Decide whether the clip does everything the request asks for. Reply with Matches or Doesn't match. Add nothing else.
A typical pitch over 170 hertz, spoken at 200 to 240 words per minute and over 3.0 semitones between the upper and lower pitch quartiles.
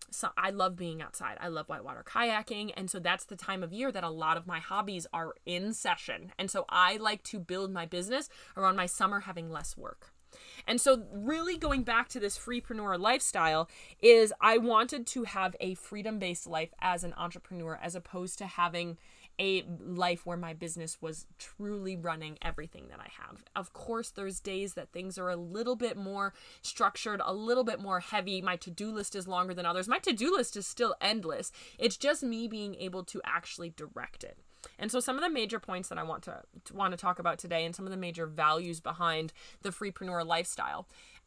Matches